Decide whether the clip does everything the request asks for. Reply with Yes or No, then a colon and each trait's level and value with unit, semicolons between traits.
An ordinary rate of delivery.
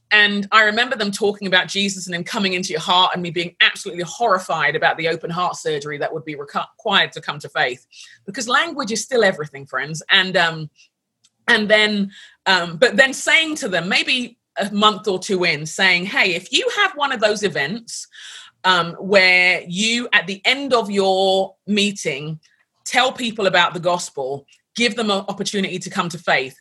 Yes: average, 190 wpm